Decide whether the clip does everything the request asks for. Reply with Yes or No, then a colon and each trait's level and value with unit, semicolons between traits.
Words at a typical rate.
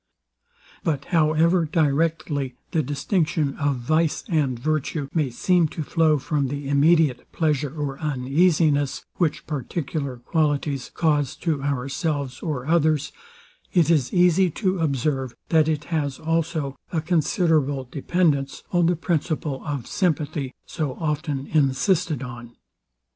No: slow, 125 wpm